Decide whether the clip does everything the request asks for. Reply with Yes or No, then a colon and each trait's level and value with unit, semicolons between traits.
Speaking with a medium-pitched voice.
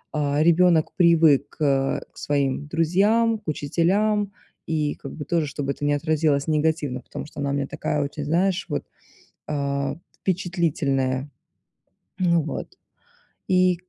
Yes: medium, 155 Hz